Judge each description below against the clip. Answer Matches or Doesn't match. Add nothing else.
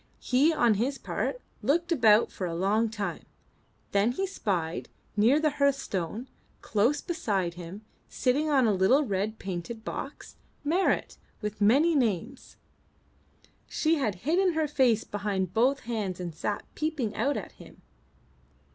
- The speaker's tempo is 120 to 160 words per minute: Matches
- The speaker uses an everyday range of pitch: Doesn't match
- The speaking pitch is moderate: Doesn't match